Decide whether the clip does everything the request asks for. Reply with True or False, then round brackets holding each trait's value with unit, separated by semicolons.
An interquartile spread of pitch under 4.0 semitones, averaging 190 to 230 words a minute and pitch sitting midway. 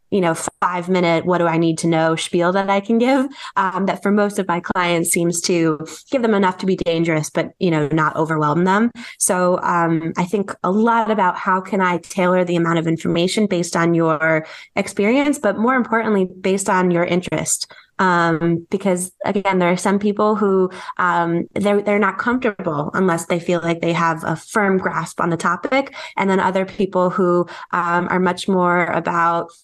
True (2.9 semitones; 195 wpm; 180 Hz)